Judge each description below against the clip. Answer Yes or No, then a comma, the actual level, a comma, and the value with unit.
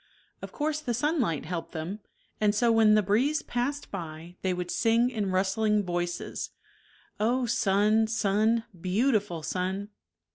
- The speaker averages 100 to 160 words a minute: Yes, average, 145 wpm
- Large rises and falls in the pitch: No, average, 4.1 semitones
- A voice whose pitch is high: Yes, high, 210 Hz